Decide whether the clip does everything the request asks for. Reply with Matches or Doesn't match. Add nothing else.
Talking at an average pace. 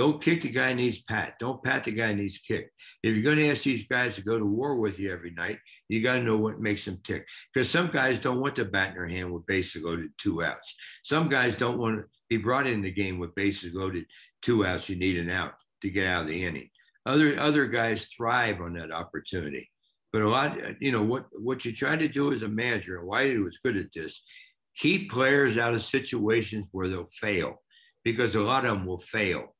Doesn't match